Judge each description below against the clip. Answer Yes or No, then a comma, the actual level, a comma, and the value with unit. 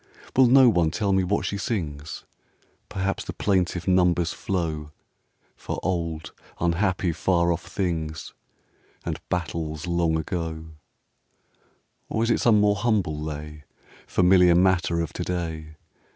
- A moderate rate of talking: No, slow, 130 wpm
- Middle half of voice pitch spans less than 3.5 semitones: Yes, average, 3.0 semitones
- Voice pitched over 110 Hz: No, very low, 85 Hz